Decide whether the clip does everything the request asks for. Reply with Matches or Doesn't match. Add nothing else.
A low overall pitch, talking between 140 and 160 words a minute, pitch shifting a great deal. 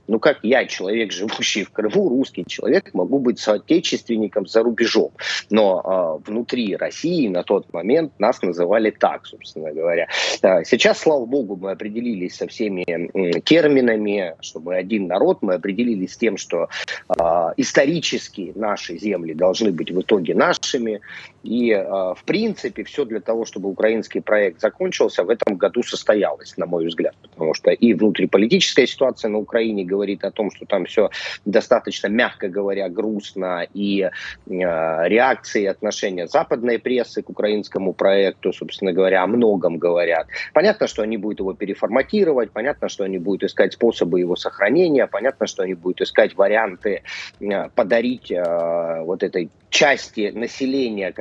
Doesn't match